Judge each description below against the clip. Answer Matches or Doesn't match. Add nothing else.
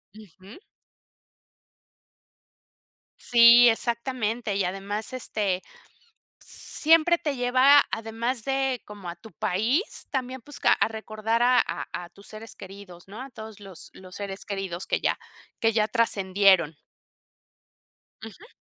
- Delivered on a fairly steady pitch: Doesn't match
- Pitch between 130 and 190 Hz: Doesn't match